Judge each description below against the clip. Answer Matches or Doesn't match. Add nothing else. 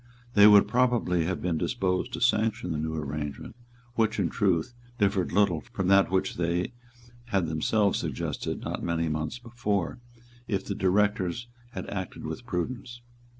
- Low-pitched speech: Matches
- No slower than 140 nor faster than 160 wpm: Matches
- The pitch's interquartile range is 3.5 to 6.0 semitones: Matches